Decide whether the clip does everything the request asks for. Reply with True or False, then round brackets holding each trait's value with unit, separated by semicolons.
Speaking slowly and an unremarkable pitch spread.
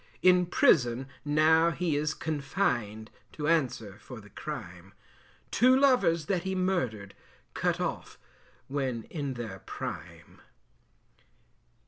False (110 wpm; 6.6 semitones)